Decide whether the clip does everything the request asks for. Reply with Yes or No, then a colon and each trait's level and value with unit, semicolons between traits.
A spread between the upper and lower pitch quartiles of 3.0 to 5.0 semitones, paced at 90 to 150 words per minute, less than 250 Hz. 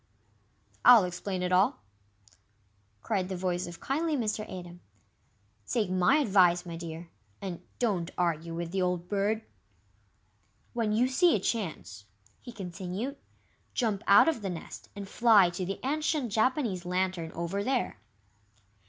Yes: average, 4.4 semitones; average, 140 wpm; high, 190 Hz